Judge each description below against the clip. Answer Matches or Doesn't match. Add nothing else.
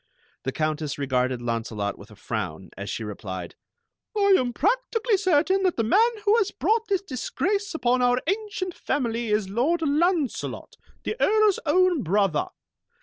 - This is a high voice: Matches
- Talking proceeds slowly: Doesn't match